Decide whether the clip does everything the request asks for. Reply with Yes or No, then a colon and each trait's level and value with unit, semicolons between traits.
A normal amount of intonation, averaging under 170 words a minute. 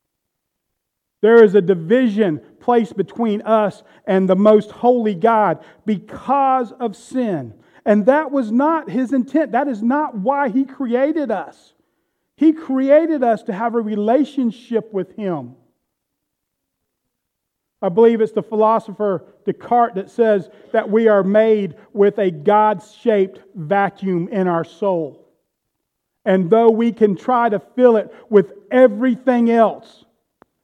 Yes: average, 3.8 semitones; slow, 135 wpm